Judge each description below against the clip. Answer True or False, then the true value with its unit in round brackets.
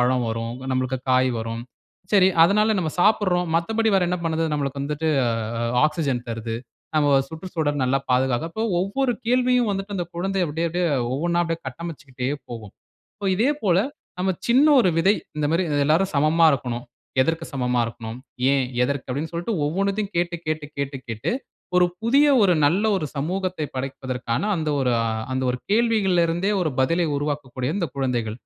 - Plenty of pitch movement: True (6.3 semitones)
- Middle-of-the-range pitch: True (160 Hz)